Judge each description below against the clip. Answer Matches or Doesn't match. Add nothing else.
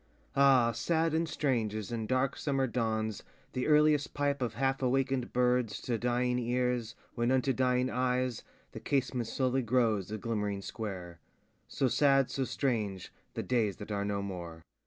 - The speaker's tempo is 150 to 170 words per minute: Matches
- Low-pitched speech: Matches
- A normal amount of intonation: Matches